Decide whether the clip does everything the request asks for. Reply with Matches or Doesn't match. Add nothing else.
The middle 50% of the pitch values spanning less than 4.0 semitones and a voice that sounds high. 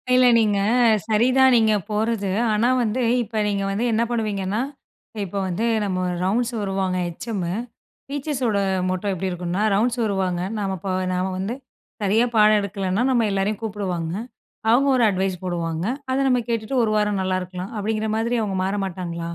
Matches